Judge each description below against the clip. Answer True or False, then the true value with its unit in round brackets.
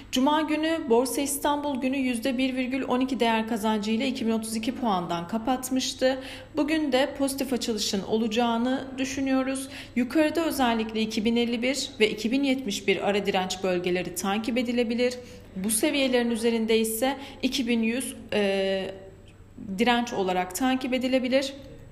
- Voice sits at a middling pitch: False (245 Hz)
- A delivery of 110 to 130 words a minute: False (100 wpm)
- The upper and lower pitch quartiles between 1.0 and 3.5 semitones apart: True (3.2 semitones)